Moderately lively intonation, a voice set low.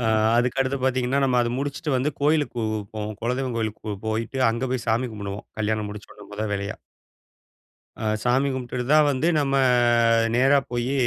Yes: average, 3.7 semitones; low, 125 Hz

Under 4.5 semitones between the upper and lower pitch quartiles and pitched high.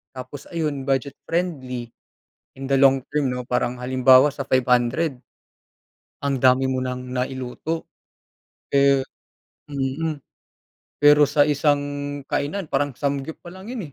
No: narrow, 2.4 semitones; medium, 140 Hz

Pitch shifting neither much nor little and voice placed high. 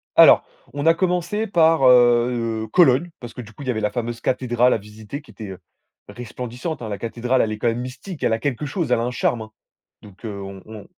No: average, 4.1 semitones; low, 120 Hz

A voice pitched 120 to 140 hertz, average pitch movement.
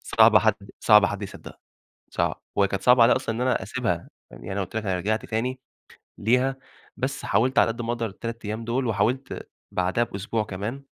No: low, 110 Hz; average, 3.5 semitones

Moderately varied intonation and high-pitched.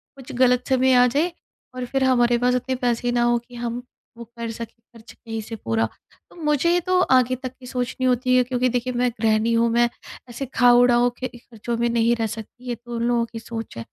No: narrow, 1.4 semitones; high, 240 Hz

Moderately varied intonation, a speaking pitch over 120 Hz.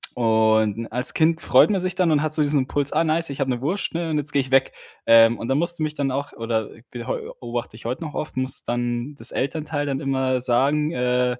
Yes: average, 3.9 semitones; low, 135 Hz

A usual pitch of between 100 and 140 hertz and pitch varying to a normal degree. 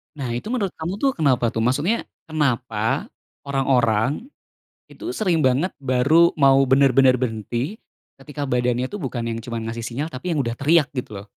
Yes: low, 135 Hz; average, 4.5 semitones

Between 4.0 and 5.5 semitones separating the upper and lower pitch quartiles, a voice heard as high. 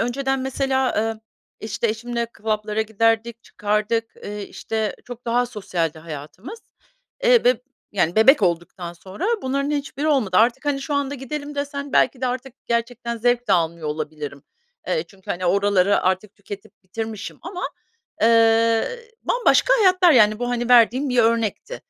Yes: average, 4.6 semitones; high, 230 Hz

